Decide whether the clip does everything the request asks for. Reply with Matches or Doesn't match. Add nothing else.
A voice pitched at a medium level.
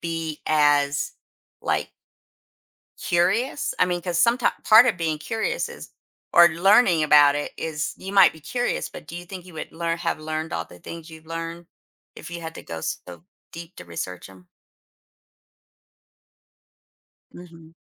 Matches